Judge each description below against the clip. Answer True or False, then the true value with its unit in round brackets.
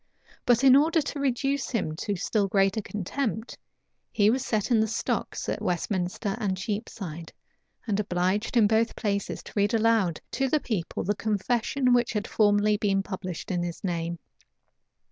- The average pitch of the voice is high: True (210 Hz)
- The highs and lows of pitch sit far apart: False (3.7 semitones)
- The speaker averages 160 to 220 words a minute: True (165 wpm)